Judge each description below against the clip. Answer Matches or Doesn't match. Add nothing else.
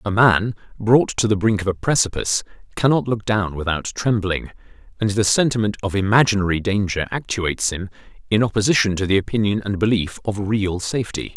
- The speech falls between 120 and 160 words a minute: Doesn't match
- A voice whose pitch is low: Matches